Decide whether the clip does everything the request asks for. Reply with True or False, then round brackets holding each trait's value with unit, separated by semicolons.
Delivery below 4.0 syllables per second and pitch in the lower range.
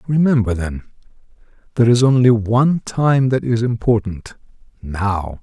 False (4.6 syllables/s; 115 Hz)